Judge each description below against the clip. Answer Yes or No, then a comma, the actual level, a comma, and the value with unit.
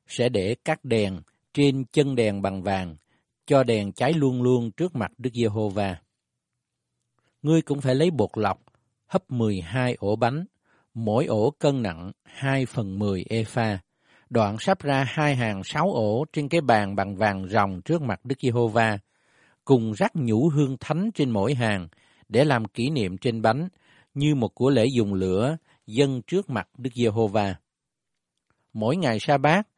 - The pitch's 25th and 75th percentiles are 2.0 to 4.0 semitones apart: No, average, 5.2 semitones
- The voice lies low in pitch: Yes, low, 120 Hz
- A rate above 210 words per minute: No, slow, 165 wpm